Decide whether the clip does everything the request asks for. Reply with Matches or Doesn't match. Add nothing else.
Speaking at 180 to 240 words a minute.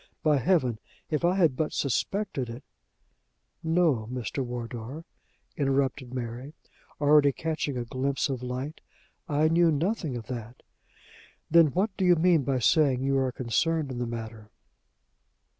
Doesn't match